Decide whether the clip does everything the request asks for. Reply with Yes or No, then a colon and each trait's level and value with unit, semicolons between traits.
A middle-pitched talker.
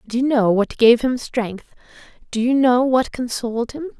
No: high, 245 Hz